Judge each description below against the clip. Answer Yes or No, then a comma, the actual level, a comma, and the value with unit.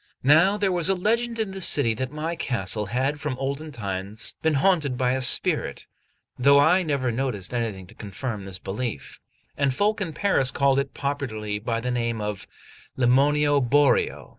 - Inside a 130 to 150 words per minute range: No, average, 175 wpm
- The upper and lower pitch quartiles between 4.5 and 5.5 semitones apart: Yes, average, 4.8 semitones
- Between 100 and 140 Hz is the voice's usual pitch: Yes, low, 135 Hz